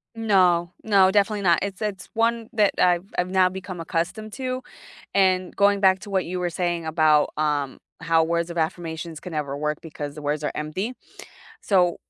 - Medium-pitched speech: Yes, medium, 180 Hz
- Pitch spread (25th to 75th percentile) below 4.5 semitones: Yes, average, 3.5 semitones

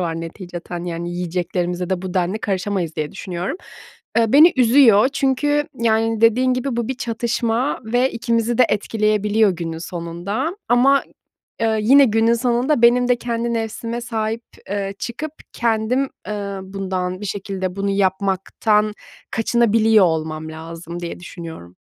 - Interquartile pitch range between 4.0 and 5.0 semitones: Yes, average, 4.7 semitones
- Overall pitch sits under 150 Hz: No, high, 215 Hz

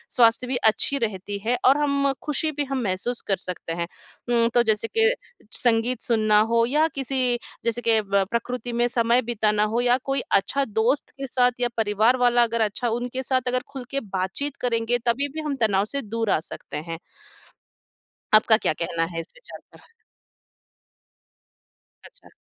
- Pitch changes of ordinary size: Yes, average, 3.1 semitones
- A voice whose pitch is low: No, high, 235 Hz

